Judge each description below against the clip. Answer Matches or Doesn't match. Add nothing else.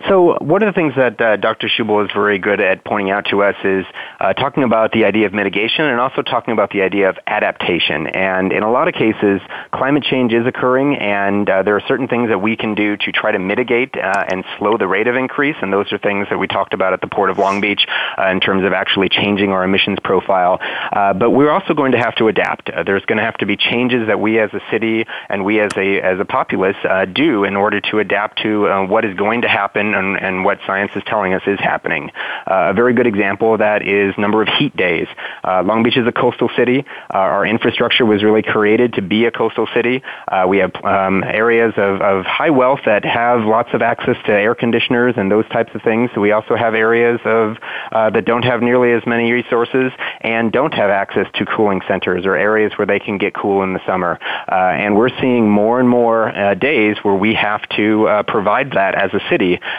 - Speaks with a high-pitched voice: Doesn't match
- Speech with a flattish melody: Doesn't match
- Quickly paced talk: Matches